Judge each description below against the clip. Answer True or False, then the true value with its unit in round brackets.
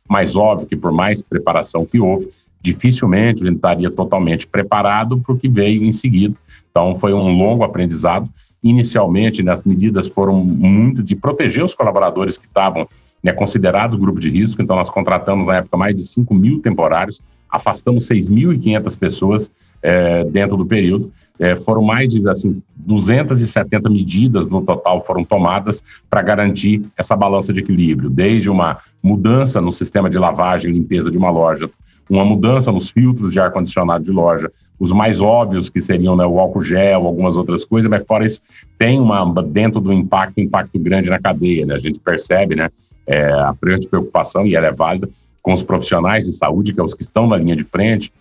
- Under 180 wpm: False (185 wpm)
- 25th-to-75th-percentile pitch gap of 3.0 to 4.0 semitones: True (3.3 semitones)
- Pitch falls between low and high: False (100 Hz)